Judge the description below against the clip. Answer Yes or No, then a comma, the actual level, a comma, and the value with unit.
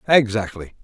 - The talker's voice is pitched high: No, low, 110 Hz